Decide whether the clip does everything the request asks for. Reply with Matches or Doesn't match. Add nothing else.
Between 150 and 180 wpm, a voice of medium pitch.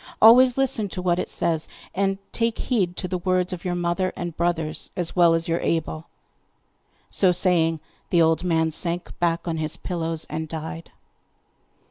Matches